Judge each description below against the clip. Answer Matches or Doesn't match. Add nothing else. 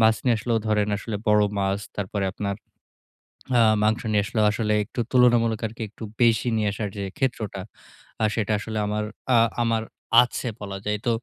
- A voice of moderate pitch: Doesn't match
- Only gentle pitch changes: Matches